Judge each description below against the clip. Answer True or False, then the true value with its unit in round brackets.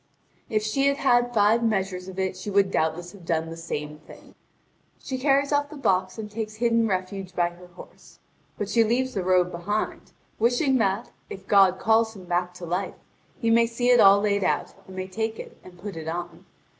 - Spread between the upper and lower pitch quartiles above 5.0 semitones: False (4.1 semitones)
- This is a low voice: False (200 Hz)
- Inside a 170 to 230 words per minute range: True (205 wpm)